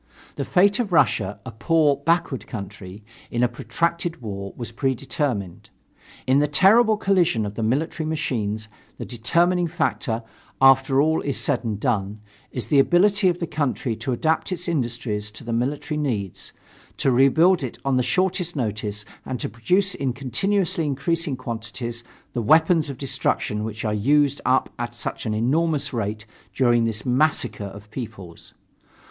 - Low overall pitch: Yes, low, 130 Hz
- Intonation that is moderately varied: No, wide, 6.0 semitones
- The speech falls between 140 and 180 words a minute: Yes, average, 160 wpm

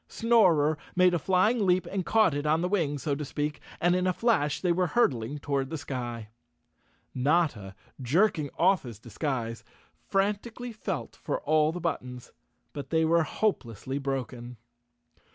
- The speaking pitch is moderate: Yes, medium, 155 Hz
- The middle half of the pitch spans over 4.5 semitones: Yes, average, 5.3 semitones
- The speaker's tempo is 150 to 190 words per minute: Yes, average, 155 wpm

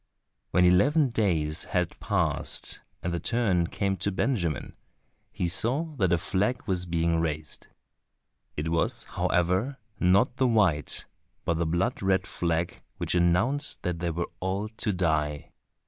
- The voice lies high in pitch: No, very low, 90 Hz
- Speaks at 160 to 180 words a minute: No, average, 145 wpm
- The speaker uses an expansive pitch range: No, average, 4.2 semitones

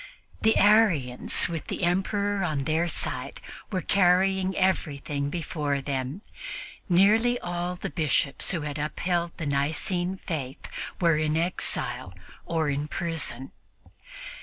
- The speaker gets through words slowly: Yes, slow, 120 wpm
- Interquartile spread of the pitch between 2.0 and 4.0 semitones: No, average, 4.4 semitones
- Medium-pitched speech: Yes, medium, 170 Hz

